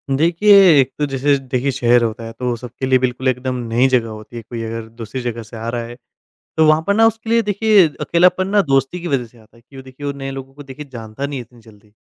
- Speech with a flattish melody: No, average, 3.8 semitones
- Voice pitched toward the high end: No, low, 130 Hz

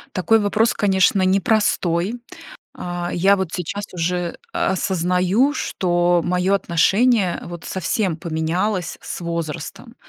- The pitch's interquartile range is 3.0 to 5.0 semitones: No, narrow, 2.5 semitones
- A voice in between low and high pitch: Yes, medium, 180 Hz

